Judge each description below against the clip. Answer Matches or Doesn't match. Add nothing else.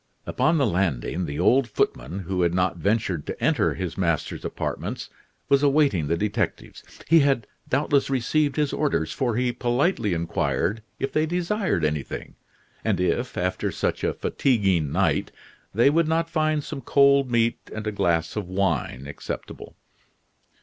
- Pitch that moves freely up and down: Matches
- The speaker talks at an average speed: Matches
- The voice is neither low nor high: Doesn't match